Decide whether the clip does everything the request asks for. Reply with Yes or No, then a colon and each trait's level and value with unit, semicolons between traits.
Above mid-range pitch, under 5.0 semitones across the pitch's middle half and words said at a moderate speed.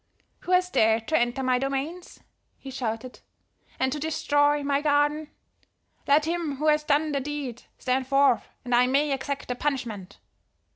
Yes: very high, 280 Hz; average, 2.8 semitones; average, 160 wpm